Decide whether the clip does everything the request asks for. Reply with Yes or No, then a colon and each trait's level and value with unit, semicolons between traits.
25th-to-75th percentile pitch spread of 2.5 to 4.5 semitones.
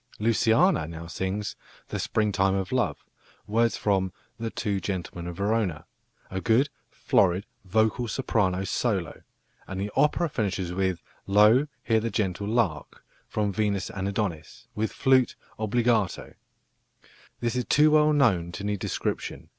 Yes: average, 3.4 semitones